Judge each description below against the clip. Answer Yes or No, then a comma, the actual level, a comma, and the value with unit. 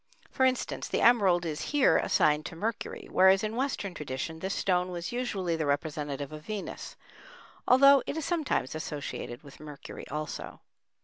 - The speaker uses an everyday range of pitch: No, wide, 7.5 semitones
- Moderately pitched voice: Yes, medium, 180 Hz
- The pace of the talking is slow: No, average, 160 wpm